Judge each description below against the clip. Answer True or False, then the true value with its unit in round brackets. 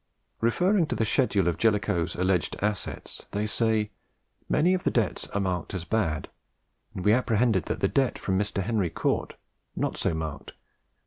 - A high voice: False (105 Hz)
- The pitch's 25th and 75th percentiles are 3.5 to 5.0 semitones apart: True (3.9 semitones)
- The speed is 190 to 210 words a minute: False (180 wpm)